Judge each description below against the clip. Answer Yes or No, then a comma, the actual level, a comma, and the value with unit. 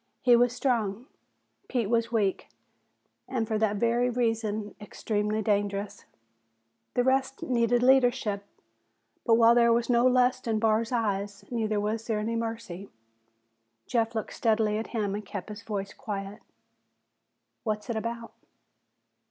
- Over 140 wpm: No, slow, 135 wpm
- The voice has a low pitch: No, high, 225 Hz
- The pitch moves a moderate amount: No, narrow, 2.2 semitones